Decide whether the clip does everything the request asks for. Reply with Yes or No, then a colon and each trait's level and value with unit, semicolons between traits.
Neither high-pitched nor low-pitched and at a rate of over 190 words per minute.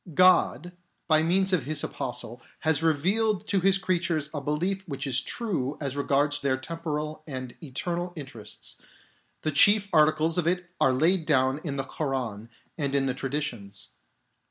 No: medium, 150 Hz; average, 160 wpm